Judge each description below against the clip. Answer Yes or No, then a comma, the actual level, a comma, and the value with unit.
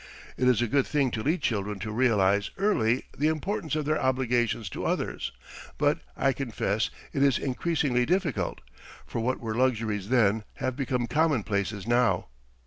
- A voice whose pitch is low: Yes, low, 125 Hz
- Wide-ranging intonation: No, average, 4.2 semitones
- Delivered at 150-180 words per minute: Yes, average, 160 wpm